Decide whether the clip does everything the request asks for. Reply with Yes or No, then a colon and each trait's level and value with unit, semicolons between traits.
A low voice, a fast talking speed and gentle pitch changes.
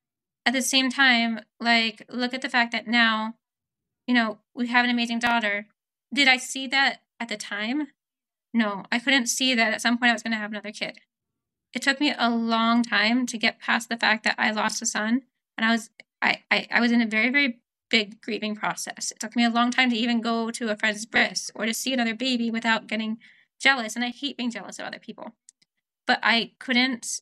No: high, 235 Hz; fast, 225 wpm; narrow, 2.0 semitones